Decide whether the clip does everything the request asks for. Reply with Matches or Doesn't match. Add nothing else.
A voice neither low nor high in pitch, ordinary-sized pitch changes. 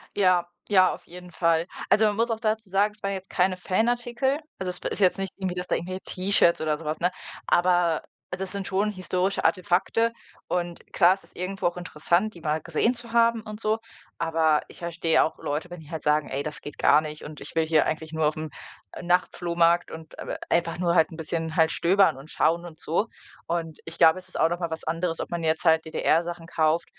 Matches